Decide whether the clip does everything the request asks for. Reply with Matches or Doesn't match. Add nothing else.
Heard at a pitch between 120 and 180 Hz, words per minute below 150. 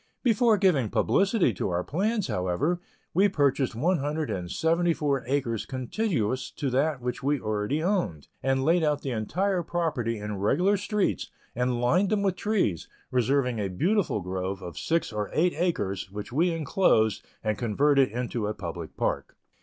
Doesn't match